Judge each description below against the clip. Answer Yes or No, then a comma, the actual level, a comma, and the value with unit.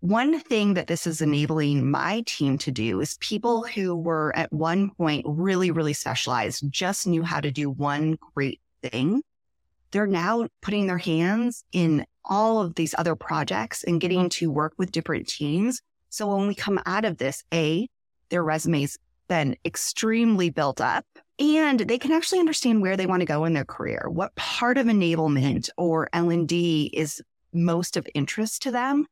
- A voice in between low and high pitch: Yes, medium, 175 Hz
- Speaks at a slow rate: No, average, 175 wpm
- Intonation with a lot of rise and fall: Yes, wide, 5.8 semitones